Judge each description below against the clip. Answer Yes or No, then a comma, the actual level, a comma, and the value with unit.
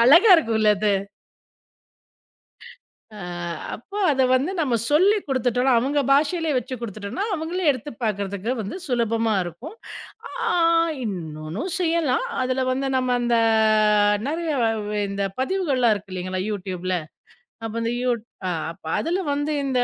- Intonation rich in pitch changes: Yes, wide, 5.9 semitones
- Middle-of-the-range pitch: No, very high, 250 Hz